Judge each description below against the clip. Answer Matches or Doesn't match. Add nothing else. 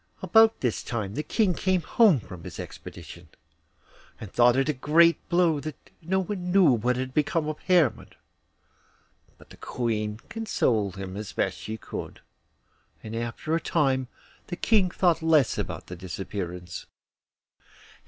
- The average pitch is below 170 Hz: Matches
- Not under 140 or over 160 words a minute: Matches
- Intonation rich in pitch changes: Matches